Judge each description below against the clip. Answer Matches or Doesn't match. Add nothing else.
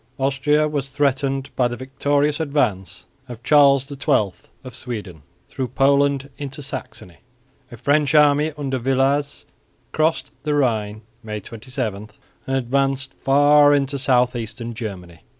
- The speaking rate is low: Matches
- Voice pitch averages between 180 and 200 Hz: Doesn't match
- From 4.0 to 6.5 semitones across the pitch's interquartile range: Doesn't match